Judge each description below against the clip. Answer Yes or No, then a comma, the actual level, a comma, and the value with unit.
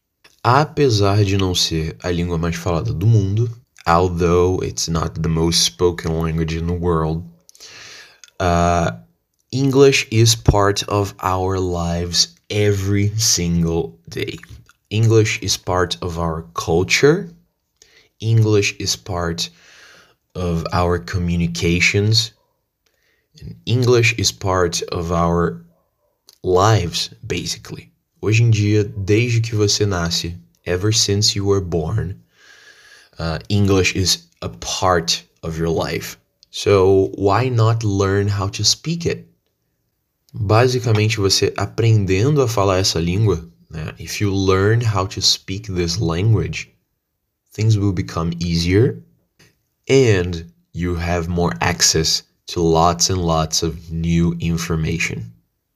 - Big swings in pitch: No, average, 3.9 semitones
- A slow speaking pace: Yes, slow, 120 wpm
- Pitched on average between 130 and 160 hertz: No, very low, 95 Hz